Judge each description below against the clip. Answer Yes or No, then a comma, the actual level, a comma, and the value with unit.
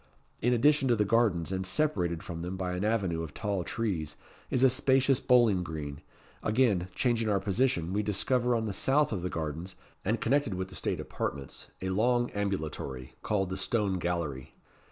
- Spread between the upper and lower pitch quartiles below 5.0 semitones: No, wide, 5.4 semitones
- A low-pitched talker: Yes, low, 100 Hz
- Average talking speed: Yes, average, 180 wpm